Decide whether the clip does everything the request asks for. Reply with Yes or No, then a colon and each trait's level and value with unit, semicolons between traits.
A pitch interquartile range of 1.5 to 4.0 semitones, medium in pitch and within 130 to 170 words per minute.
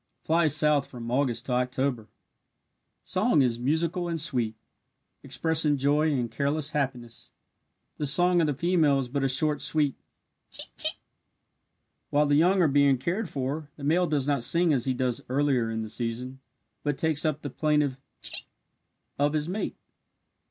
Yes: average, 3.3 semitones; medium, 145 Hz; average, 165 wpm